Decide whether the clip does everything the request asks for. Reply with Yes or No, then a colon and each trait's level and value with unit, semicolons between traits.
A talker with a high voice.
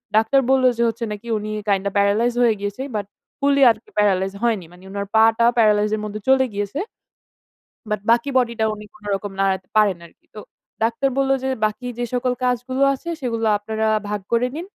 Yes: high, 220 Hz